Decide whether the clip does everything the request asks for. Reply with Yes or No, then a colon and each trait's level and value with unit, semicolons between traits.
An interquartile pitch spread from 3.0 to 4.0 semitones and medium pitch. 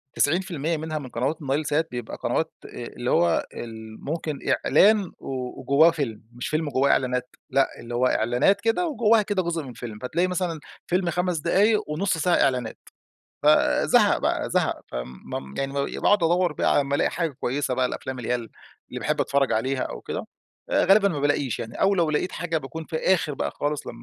No: wide, 5.4 semitones; medium, 150 Hz